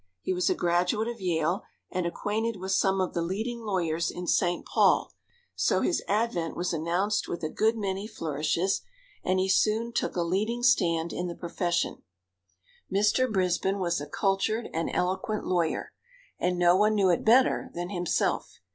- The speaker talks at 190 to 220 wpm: No, average, 170 wpm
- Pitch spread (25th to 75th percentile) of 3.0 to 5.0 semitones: Yes, average, 3.5 semitones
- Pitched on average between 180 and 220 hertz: Yes, medium, 185 Hz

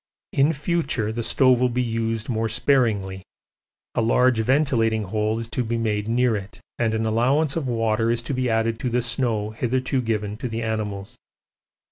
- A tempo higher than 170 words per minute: Yes, average, 180 wpm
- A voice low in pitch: Yes, low, 115 Hz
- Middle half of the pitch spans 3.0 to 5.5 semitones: No, narrow, 2.4 semitones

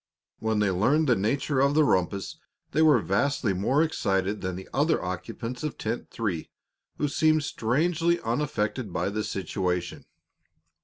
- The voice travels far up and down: Yes, wide, 7.0 semitones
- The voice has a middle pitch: No, low, 115 Hz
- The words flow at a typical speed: Yes, average, 150 wpm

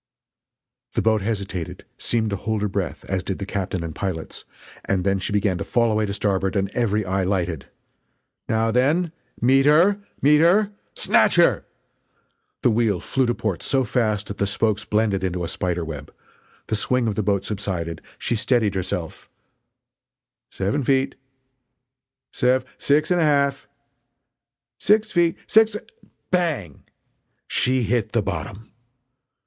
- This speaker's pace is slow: No, average, 155 wpm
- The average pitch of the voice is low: Yes, low, 110 Hz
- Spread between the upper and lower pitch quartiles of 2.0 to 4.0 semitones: No, average, 5.1 semitones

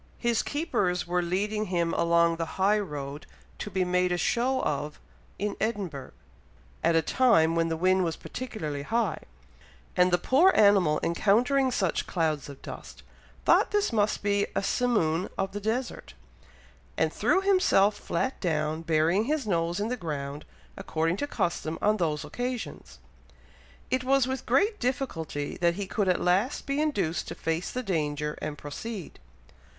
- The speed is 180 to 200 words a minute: No, average, 160 wpm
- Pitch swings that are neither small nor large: No, wide, 6.3 semitones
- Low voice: No, medium, 185 Hz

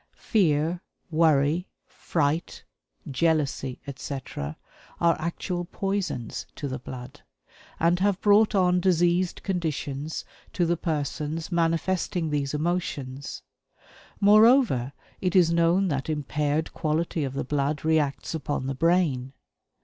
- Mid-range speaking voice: Yes, medium, 160 Hz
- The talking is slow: Yes, slow, 110 wpm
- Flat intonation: No, average, 3.8 semitones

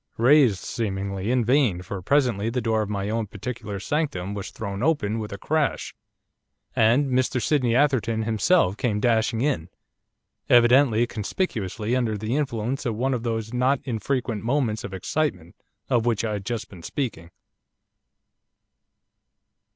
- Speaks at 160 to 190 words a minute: No, average, 145 wpm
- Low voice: Yes, low, 115 Hz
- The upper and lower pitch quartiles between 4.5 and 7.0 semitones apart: No, average, 3.8 semitones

